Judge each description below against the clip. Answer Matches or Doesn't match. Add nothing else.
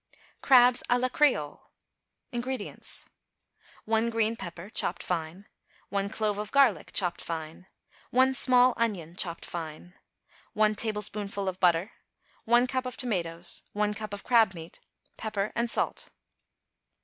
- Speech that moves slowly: Matches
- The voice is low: Doesn't match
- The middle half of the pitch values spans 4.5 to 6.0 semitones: Matches